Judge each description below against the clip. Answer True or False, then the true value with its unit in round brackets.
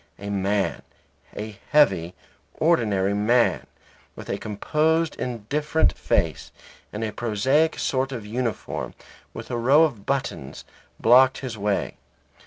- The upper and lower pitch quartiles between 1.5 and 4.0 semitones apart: False (5.1 semitones)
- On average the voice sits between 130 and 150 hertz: False (120 Hz)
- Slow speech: True (120 wpm)